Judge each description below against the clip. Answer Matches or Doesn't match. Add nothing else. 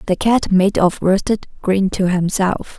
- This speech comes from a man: Doesn't match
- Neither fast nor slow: Matches